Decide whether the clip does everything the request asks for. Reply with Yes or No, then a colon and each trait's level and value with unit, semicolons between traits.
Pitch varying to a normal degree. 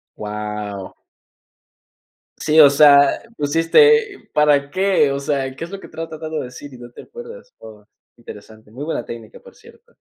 No: wide, 6.3 semitones